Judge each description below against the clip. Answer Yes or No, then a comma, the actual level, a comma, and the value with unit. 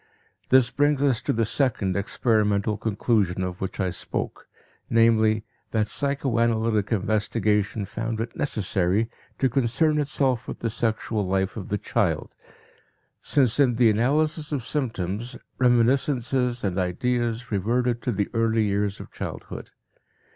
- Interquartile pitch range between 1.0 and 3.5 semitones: Yes, average, 3.2 semitones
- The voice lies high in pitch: No, low, 115 Hz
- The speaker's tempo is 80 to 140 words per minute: Yes, slow, 135 wpm